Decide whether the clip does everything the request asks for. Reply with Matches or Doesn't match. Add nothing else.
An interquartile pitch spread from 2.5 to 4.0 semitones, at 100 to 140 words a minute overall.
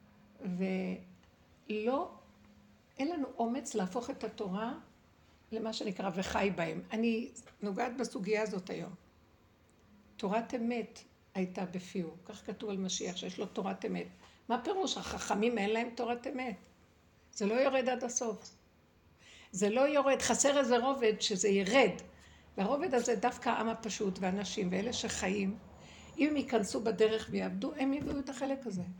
Doesn't match